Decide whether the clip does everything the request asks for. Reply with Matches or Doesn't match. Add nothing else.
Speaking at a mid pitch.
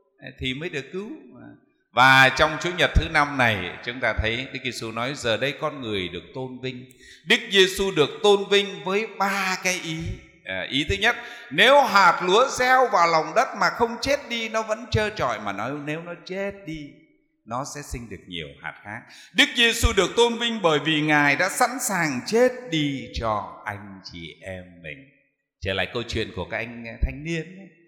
Matches